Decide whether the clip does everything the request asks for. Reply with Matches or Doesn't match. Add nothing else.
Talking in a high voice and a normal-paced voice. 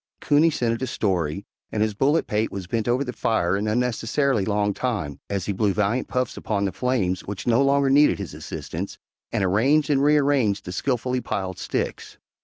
Doesn't match